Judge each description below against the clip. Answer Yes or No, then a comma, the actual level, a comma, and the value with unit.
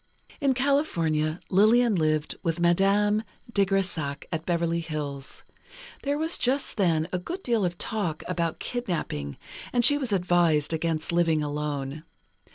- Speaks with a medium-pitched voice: Yes, medium, 175 Hz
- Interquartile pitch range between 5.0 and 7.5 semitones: Yes, wide, 5.4 semitones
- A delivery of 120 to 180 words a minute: Yes, average, 140 wpm